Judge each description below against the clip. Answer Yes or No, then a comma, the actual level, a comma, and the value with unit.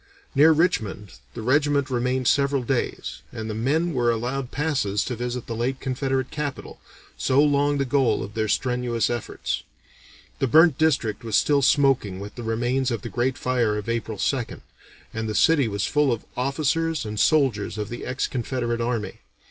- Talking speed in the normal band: Yes, average, 175 wpm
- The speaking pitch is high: No, low, 125 Hz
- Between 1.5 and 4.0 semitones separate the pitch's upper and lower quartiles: Yes, average, 3.7 semitones